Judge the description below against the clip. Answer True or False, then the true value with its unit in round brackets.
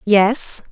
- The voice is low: False (215 Hz)